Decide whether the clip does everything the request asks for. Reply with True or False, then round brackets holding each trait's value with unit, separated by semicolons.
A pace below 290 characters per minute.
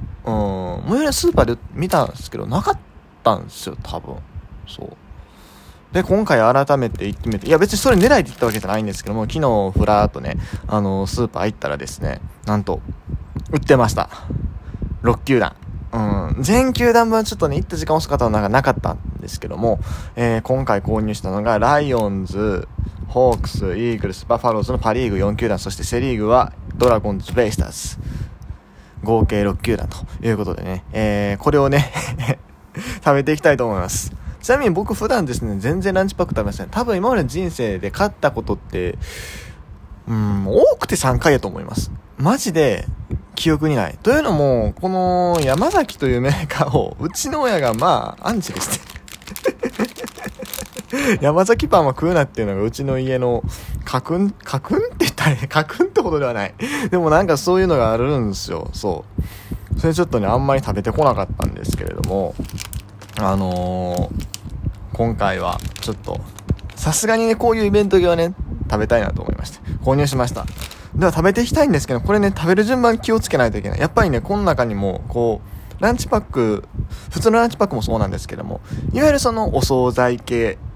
False (375 characters per minute)